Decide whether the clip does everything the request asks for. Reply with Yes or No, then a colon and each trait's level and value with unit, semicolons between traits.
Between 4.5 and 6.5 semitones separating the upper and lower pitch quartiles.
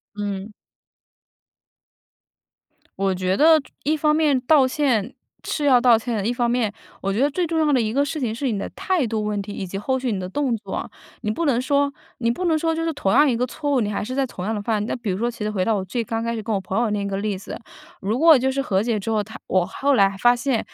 Yes: average, 5.2 semitones